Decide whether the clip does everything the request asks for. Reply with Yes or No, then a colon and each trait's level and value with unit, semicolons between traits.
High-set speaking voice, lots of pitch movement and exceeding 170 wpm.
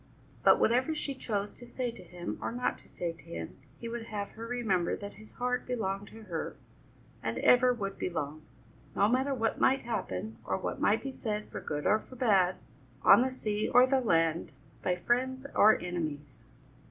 Yes: high, 215 Hz; wide, 5.7 semitones; average, 190 wpm